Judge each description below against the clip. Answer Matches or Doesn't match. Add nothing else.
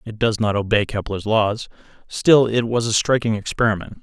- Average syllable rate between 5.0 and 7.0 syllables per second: Matches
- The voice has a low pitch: Matches